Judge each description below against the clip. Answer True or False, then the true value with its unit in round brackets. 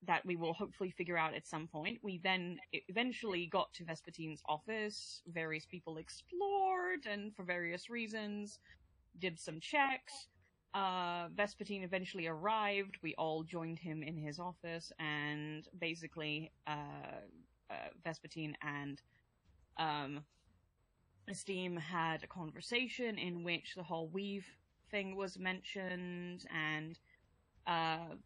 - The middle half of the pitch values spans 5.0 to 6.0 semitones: False (3.8 semitones)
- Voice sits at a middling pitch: True (175 Hz)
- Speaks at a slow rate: True (125 wpm)